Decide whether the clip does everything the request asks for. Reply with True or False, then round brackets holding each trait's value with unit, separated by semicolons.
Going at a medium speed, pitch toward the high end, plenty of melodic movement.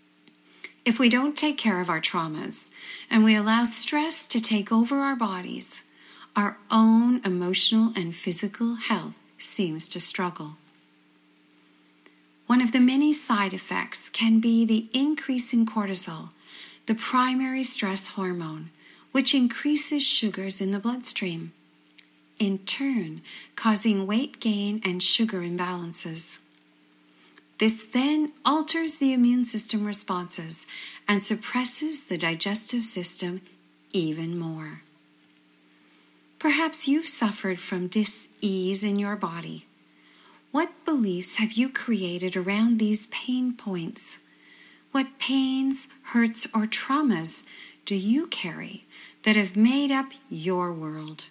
False (120 wpm; 210 Hz; 6.2 semitones)